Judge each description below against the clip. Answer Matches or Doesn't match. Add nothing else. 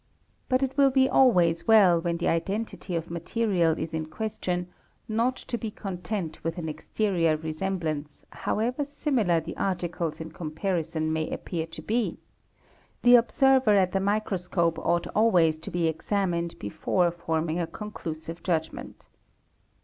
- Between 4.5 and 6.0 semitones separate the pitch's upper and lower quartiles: Matches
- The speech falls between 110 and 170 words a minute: Matches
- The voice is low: Doesn't match